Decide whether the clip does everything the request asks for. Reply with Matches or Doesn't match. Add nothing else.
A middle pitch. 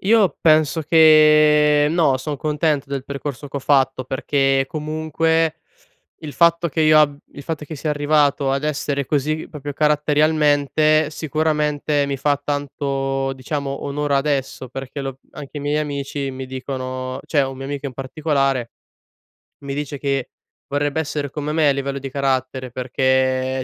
Matches